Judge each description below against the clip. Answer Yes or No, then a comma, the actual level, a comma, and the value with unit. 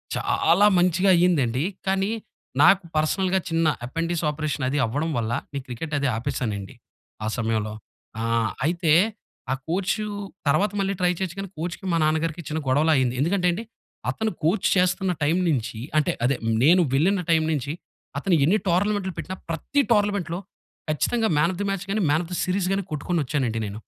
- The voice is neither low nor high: Yes, medium, 165 Hz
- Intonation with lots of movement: No, average, 4.8 semitones